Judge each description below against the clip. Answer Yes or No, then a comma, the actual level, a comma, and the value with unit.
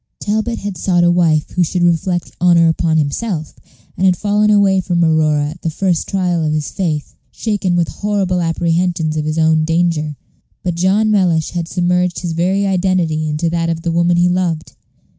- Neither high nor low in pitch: Yes, medium, 175 Hz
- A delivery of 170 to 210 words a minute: Yes, average, 185 wpm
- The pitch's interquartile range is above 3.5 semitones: No, narrow, 2.4 semitones